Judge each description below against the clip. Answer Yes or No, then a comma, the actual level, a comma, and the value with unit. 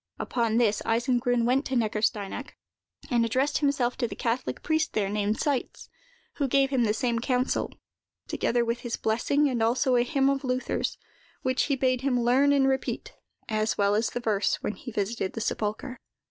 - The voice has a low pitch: No, high, 245 Hz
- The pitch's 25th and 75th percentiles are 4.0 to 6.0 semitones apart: No, average, 2.9 semitones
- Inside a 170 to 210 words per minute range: Yes, average, 180 wpm